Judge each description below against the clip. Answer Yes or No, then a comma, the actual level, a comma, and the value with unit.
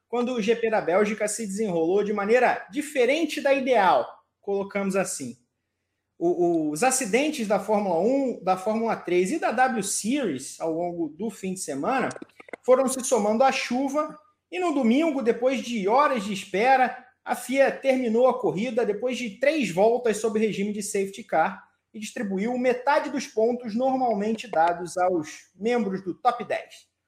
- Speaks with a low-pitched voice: No, high, 235 Hz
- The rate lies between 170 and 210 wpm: No, average, 160 wpm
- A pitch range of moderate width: Yes, average, 4.5 semitones